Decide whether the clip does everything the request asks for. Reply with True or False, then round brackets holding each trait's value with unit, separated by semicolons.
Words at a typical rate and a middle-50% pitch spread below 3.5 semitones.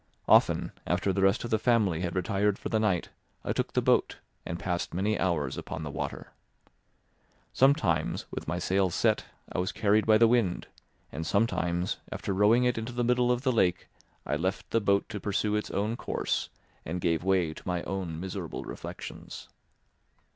False (180 wpm; 4.0 semitones)